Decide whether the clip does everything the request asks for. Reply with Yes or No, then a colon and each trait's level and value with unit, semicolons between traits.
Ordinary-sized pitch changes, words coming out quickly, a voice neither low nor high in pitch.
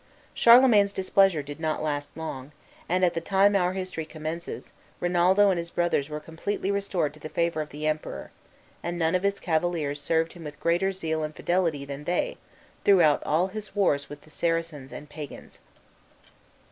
No: average, 3.5 semitones; average, 175 wpm; medium, 170 Hz